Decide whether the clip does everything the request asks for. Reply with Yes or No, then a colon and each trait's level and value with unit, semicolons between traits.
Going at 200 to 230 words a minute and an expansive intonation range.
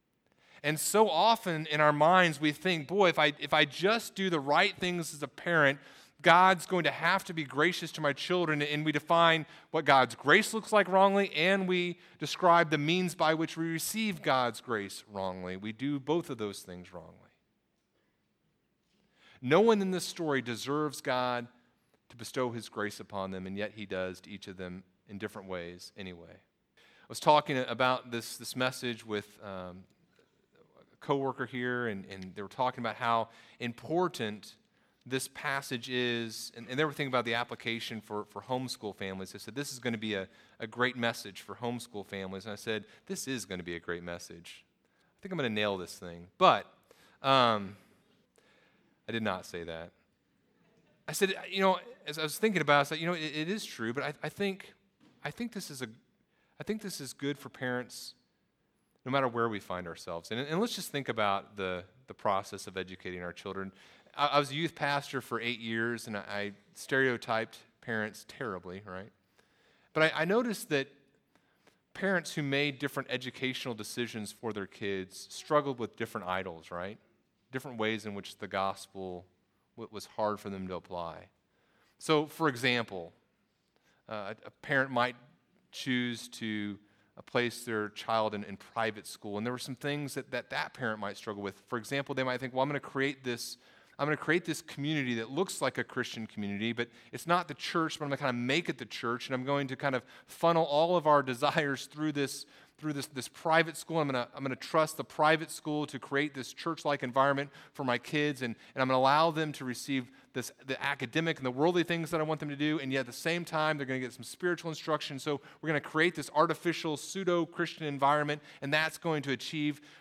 Yes: fast, 205 wpm; wide, 6.0 semitones